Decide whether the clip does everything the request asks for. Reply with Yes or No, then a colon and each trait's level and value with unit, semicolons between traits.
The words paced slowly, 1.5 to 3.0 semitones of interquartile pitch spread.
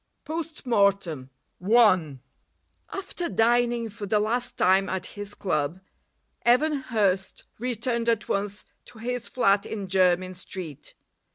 No: slow, 120 wpm; average, 4.2 semitones